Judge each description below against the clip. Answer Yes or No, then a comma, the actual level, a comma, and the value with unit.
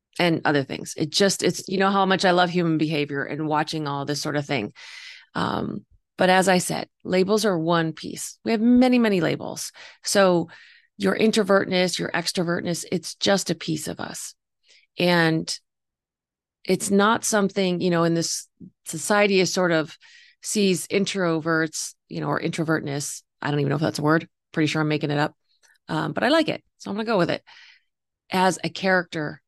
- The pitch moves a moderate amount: Yes, average, 3.8 semitones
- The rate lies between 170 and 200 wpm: Yes, average, 190 wpm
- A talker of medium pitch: Yes, medium, 180 Hz